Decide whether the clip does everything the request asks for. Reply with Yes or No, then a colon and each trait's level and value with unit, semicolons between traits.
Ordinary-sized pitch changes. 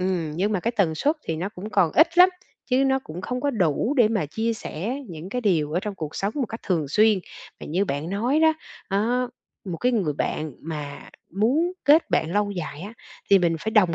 No: wide, 6.5 semitones